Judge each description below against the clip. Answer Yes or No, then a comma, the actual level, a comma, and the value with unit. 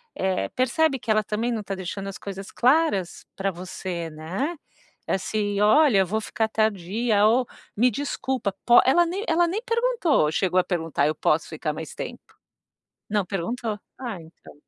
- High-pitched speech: Yes, high, 210 Hz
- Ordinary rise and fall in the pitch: No, wide, 5.7 semitones